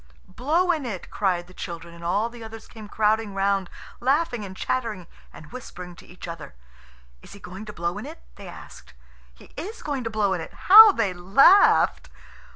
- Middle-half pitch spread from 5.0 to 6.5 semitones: Yes, wide, 5.6 semitones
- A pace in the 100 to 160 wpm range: No, average, 190 wpm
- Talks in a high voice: Yes, high, 205 Hz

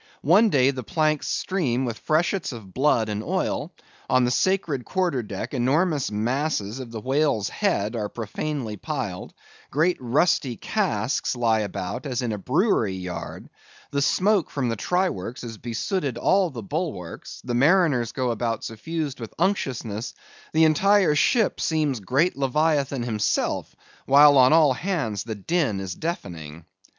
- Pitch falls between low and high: No, low, 130 Hz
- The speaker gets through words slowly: No, average, 150 wpm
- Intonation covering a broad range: Yes, wide, 6.0 semitones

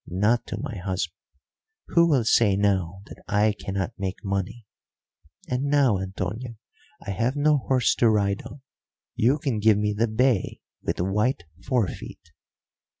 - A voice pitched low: Yes, low, 110 Hz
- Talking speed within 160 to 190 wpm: No, average, 150 wpm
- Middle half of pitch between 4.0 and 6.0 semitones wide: Yes, average, 4.5 semitones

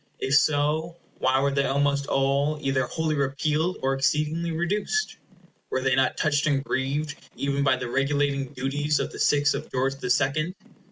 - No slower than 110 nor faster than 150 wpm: No, average, 170 wpm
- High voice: No, medium, 140 Hz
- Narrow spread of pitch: Yes, narrow, 2.1 semitones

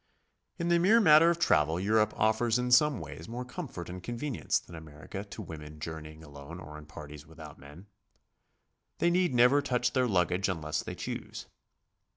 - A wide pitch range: Yes, wide, 8.5 semitones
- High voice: No, low, 100 Hz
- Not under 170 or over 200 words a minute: Yes, average, 180 wpm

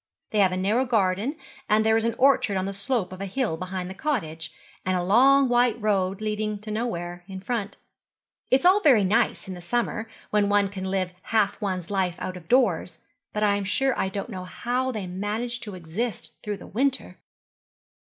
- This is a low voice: No, high, 205 Hz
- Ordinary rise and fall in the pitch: Yes, average, 4.2 semitones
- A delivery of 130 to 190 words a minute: No, fast, 205 wpm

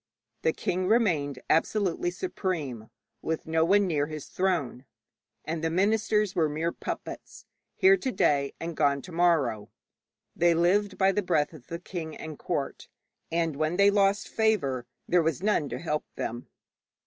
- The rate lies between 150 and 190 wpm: Yes, average, 160 wpm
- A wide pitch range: No, average, 4.2 semitones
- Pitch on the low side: No, medium, 170 Hz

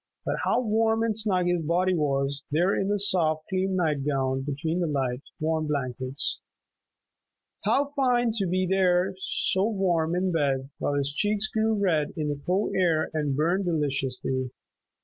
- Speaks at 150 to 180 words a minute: Yes, average, 165 wpm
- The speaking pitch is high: No, medium, 170 Hz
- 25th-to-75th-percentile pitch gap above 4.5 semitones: Yes, average, 5.1 semitones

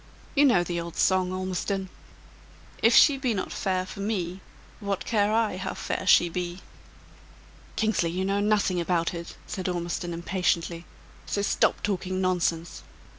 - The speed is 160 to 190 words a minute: No, average, 150 wpm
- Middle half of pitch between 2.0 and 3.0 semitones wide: Yes, narrow, 2.6 semitones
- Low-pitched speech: No, medium, 185 Hz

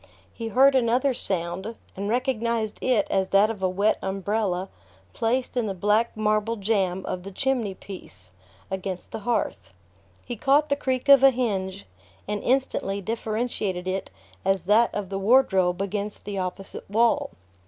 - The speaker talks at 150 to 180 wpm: Yes, average, 155 wpm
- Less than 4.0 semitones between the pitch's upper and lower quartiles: Yes, average, 3.6 semitones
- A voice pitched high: Yes, high, 210 Hz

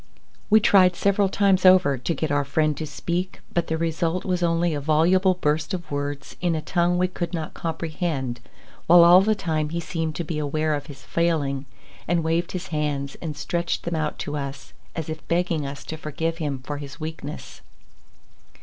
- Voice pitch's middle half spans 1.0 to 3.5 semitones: Yes, average, 2.8 semitones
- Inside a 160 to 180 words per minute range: No, average, 195 wpm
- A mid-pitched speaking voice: Yes, medium, 160 Hz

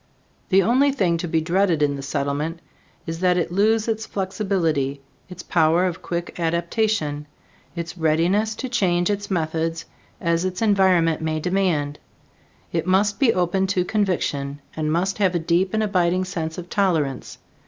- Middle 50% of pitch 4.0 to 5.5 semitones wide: No, average, 3.2 semitones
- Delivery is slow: No, average, 160 wpm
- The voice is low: No, medium, 175 Hz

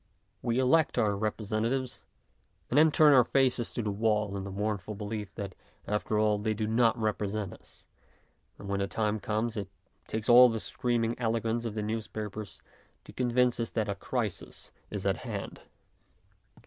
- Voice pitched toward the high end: No, low, 110 Hz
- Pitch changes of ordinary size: No, narrow, 2.2 semitones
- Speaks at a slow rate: No, average, 175 wpm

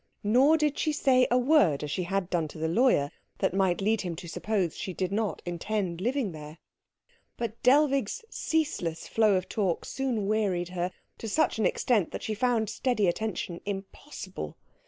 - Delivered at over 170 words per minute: Yes, average, 180 wpm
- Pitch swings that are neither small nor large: No, wide, 5.9 semitones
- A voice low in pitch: No, high, 205 Hz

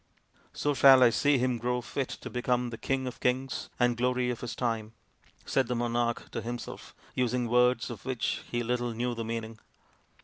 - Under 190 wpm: No, average, 195 wpm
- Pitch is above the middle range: No, low, 125 Hz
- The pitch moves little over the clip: Yes, narrow, 1.2 semitones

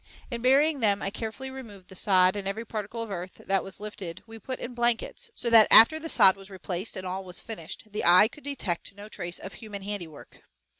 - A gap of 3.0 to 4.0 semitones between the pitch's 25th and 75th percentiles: Yes, average, 3.5 semitones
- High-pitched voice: Yes, high, 210 Hz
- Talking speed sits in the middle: No, fast, 220 wpm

